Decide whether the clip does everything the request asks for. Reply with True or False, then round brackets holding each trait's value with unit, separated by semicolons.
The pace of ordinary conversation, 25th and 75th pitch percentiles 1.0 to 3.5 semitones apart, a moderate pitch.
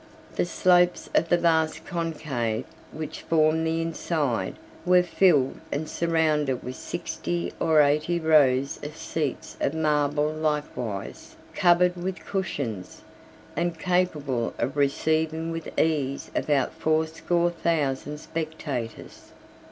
False (115 wpm; 2.9 semitones; 155 Hz)